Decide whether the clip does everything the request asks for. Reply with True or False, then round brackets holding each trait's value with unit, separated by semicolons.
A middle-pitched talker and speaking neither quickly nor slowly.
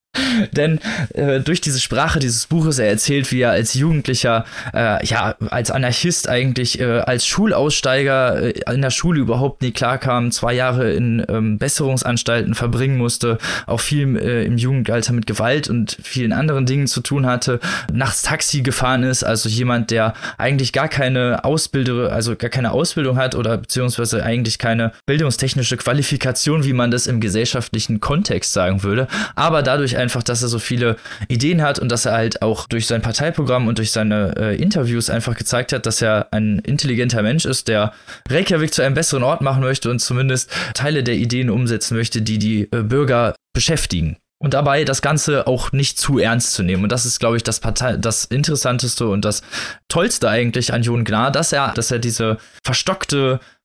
False (125 Hz; 180 wpm)